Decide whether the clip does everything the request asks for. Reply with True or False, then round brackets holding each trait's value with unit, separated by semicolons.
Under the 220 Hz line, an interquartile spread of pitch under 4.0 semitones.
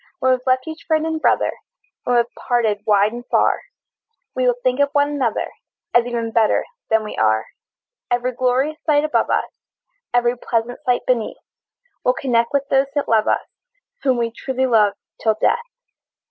False (245 Hz; 2.8 semitones)